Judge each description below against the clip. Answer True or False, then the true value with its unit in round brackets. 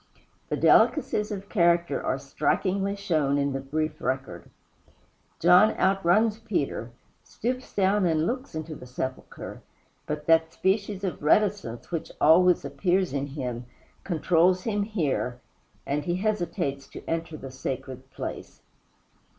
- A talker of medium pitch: True (165 Hz)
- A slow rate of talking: True (125 wpm)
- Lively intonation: True (5.8 semitones)